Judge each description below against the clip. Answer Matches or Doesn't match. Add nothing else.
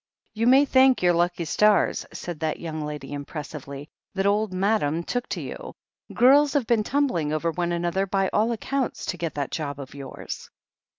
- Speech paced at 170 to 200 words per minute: Matches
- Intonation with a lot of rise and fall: Matches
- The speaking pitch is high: Doesn't match